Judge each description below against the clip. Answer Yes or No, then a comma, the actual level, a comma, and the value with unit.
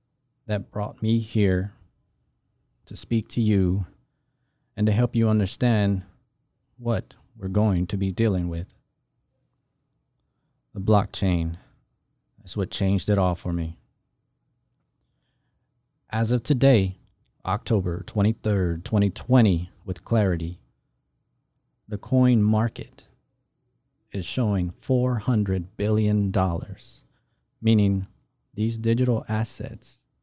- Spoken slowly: Yes, slow, 95 wpm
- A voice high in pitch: No, low, 105 Hz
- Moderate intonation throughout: Yes, average, 3.7 semitones